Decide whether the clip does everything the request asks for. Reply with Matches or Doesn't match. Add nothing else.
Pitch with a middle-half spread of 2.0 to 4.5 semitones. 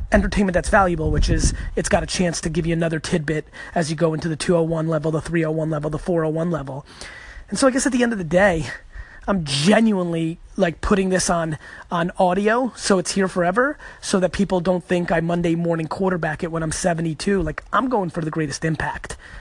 Matches